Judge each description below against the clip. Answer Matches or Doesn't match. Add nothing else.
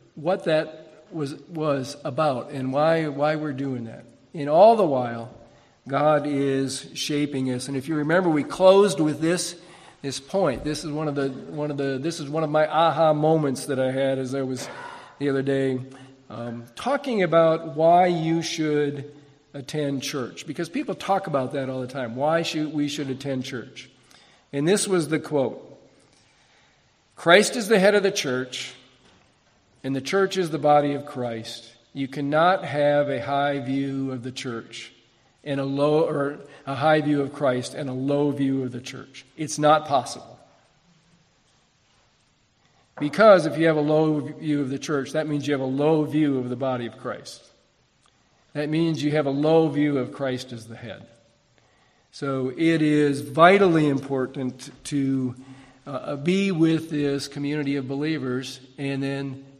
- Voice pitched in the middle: Matches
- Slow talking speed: Doesn't match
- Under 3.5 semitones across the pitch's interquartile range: Matches